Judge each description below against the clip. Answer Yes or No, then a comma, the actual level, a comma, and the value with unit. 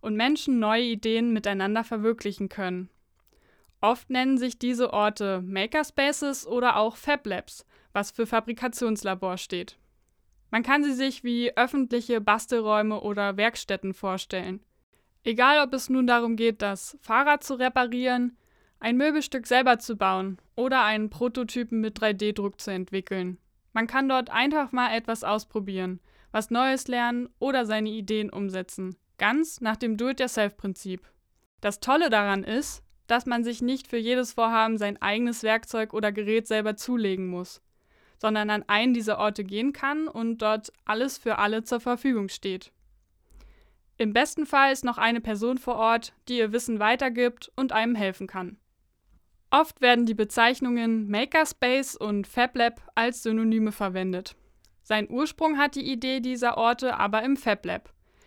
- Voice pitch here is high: Yes, high, 230 Hz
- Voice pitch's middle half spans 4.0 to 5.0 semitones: No, average, 3.3 semitones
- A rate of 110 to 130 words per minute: No, average, 145 wpm